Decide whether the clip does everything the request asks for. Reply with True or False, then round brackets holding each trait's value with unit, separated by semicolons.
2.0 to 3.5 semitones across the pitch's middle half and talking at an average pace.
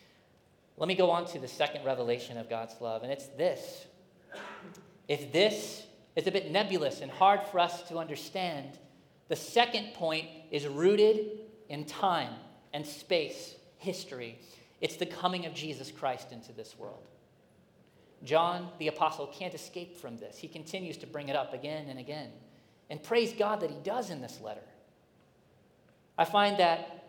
False (4.2 semitones; 160 wpm)